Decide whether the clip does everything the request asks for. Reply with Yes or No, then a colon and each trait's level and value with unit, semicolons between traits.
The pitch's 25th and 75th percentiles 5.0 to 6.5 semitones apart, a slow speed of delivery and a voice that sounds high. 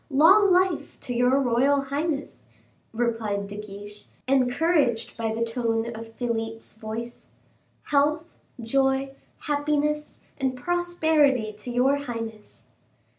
No: average, 4.3 semitones; slow, 110 wpm; very high, 250 Hz